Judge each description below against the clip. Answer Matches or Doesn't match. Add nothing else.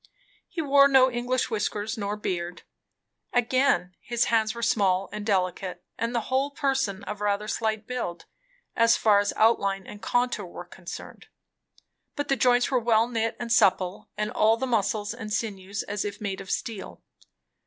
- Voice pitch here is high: Matches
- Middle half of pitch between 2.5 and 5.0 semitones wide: Matches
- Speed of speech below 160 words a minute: Doesn't match